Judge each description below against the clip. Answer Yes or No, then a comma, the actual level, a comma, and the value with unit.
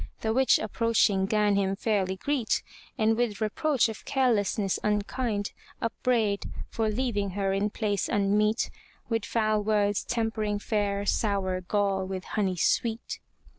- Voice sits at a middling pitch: No, high, 210 Hz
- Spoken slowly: Yes, slow, 130 wpm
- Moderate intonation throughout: No, narrow, 2.0 semitones